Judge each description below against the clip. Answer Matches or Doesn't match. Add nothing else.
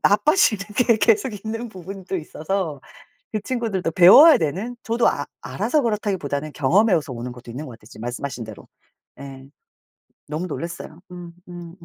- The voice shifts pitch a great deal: Matches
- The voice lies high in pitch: Doesn't match